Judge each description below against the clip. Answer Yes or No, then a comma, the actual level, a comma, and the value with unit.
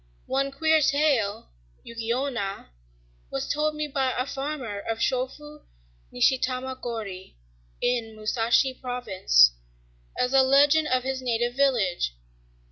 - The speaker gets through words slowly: Yes, slow, 120 wpm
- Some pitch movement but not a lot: Yes, average, 3.5 semitones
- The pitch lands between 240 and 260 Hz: Yes, very high, 255 Hz